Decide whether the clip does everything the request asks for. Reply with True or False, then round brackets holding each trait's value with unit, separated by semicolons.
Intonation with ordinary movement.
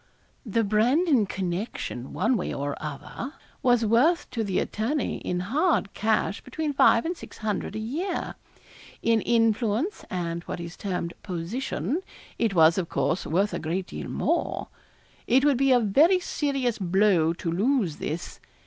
False (6.7 semitones)